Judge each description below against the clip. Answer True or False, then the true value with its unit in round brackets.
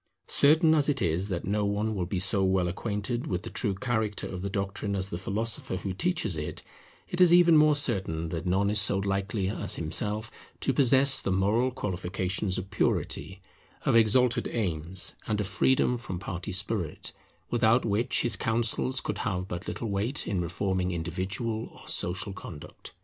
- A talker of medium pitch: False (100 Hz)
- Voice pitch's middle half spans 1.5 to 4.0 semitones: True (3.7 semitones)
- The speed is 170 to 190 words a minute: True (175 wpm)